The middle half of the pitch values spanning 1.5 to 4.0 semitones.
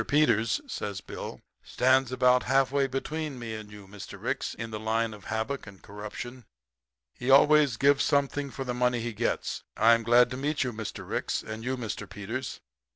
Yes: average, 3.4 semitones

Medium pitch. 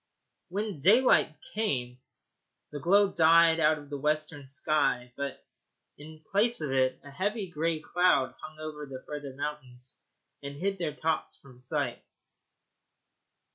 Yes: medium, 150 Hz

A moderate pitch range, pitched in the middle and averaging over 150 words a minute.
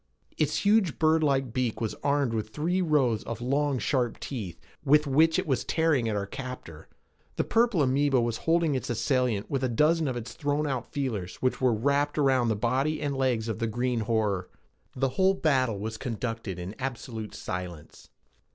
No: average, 4.5 semitones; low, 130 Hz; average, 180 wpm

